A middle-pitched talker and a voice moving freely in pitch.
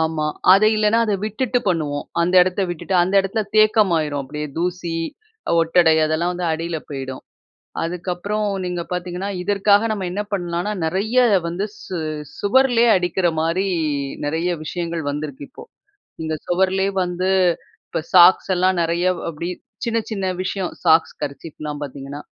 No: medium, 180 Hz; average, 3.3 semitones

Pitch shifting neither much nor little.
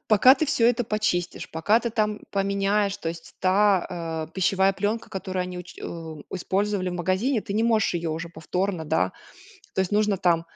Yes: average, 3.5 semitones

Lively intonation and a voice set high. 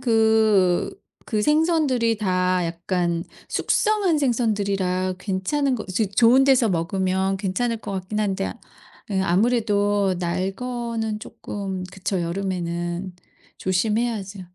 No: average, 3.9 semitones; high, 200 Hz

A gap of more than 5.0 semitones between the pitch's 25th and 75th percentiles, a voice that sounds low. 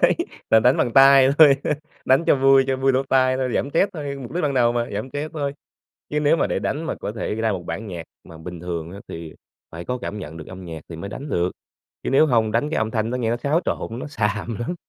Yes: wide, 5.6 semitones; low, 120 Hz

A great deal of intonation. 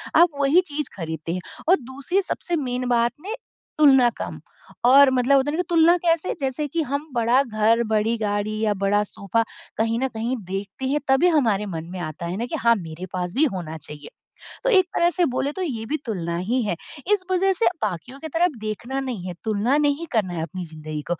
Yes: wide, 6.8 semitones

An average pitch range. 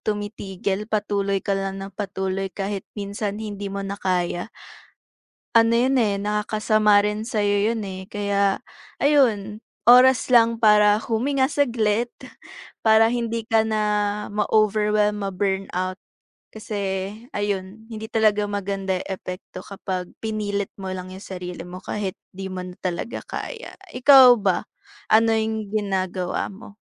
No: narrow, 2.2 semitones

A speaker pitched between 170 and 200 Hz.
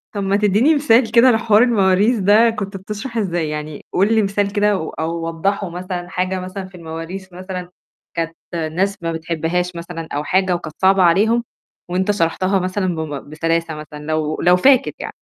Yes: medium, 185 Hz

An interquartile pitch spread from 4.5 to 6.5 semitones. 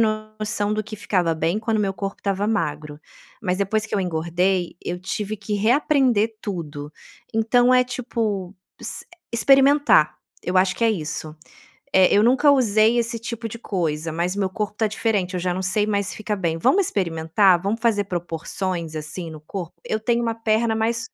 No: average, 4.0 semitones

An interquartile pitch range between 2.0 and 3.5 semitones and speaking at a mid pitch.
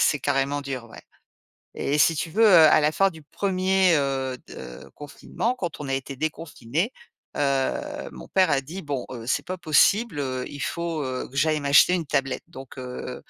No: average, 4.5 semitones; medium, 145 Hz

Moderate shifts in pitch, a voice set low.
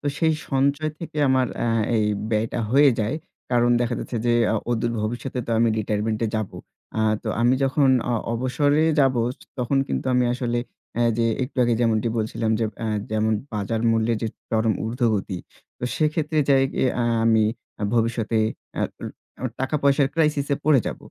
Yes: average, 3.4 semitones; low, 120 Hz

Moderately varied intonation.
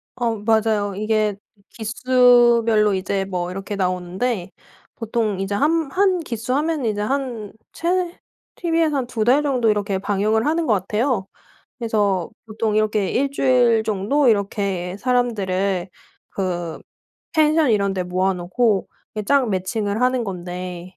Yes: average, 4.4 semitones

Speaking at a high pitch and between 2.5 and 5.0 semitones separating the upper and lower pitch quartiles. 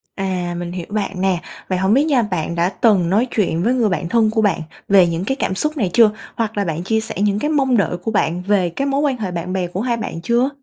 Yes: high, 200 Hz; average, 4.6 semitones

